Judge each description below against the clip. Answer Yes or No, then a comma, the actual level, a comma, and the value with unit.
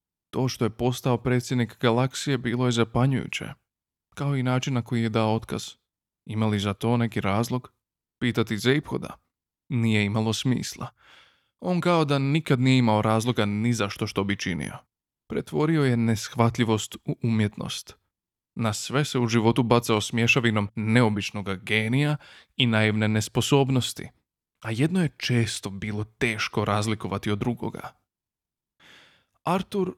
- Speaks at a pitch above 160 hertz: No, low, 115 Hz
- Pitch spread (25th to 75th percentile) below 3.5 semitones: Yes, average, 2.9 semitones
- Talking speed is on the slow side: No, average, 135 wpm